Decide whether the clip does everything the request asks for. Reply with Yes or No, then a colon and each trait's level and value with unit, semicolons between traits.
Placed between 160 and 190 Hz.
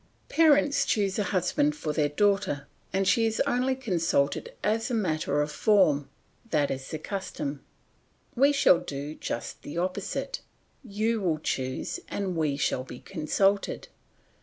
Yes: medium, 185 Hz